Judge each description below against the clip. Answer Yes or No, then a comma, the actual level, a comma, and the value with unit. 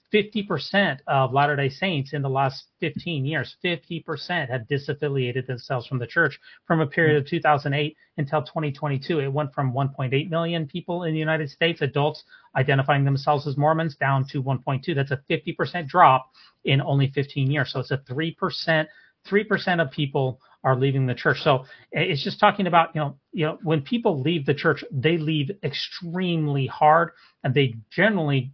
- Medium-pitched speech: Yes, medium, 150 Hz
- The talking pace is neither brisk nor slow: Yes, average, 170 wpm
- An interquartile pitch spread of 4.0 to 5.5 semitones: No, average, 3.4 semitones